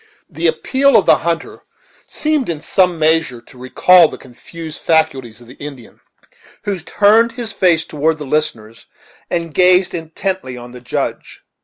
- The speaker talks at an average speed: Yes, average, 155 wpm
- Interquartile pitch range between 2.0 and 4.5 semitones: No, wide, 5.5 semitones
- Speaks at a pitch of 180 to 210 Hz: No, medium, 160 Hz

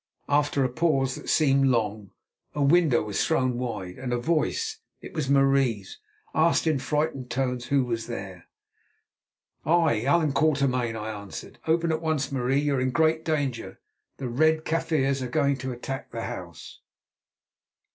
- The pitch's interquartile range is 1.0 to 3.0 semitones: No, average, 4.2 semitones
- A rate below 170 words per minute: Yes, average, 150 wpm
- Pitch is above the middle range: No, low, 135 Hz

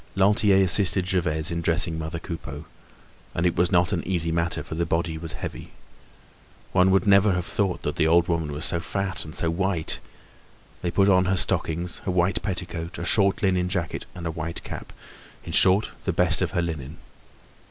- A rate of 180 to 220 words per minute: Yes, average, 185 wpm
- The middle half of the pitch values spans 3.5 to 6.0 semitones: No, narrow, 2.4 semitones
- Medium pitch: No, very low, 85 Hz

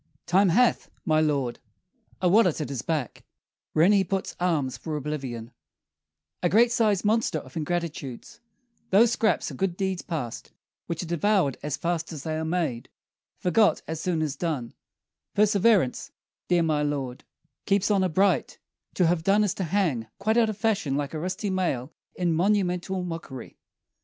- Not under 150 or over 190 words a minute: Yes, average, 160 wpm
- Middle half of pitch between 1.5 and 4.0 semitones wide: No, average, 4.6 semitones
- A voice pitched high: No, medium, 175 Hz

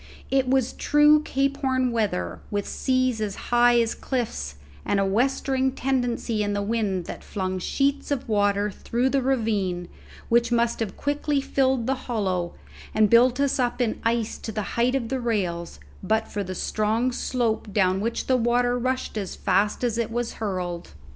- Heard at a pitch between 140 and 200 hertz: No, high, 235 Hz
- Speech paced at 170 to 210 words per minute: Yes, average, 175 wpm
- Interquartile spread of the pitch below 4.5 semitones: Yes, average, 4.0 semitones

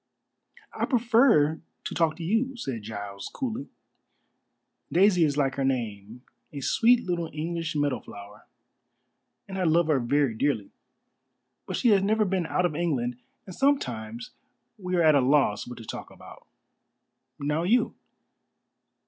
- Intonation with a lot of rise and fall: Yes, wide, 7.4 semitones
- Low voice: No, medium, 155 Hz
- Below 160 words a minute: Yes, average, 150 wpm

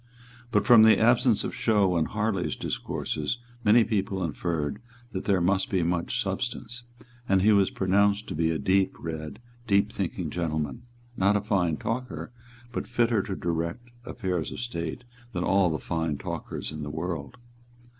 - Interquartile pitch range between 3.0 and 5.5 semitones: Yes, average, 4.5 semitones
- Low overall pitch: Yes, very low, 95 Hz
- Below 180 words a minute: Yes, average, 165 wpm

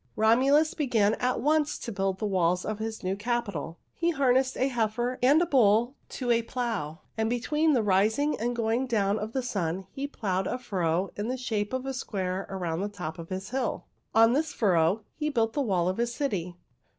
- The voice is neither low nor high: No, high, 225 Hz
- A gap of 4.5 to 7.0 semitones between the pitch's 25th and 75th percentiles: Yes, average, 4.9 semitones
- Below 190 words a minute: No, fast, 205 wpm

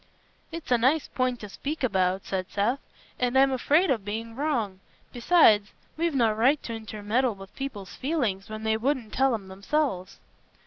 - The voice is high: Yes, high, 235 Hz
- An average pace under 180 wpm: Yes, average, 170 wpm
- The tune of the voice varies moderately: Yes, average, 4.8 semitones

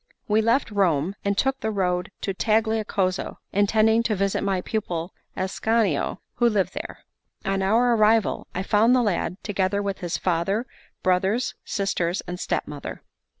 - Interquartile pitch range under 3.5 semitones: Yes, average, 3.0 semitones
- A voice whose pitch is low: No, high, 200 Hz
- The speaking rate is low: No, average, 150 wpm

